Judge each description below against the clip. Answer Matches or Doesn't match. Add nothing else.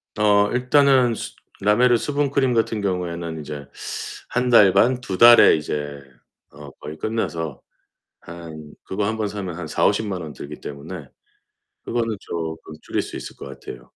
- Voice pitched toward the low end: Matches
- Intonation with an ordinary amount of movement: Doesn't match